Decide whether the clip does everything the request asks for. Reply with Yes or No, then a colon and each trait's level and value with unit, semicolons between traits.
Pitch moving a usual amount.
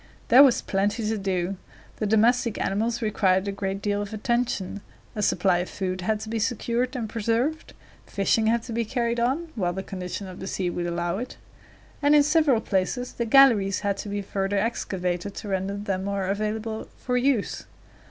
Yes: average, 3.4 semitones